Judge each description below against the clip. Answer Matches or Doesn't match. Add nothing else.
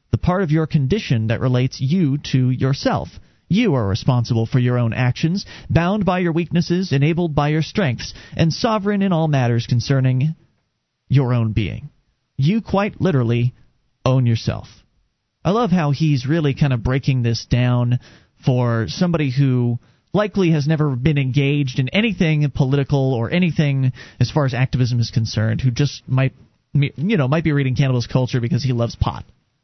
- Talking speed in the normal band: Matches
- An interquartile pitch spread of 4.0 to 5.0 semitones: Matches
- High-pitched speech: Doesn't match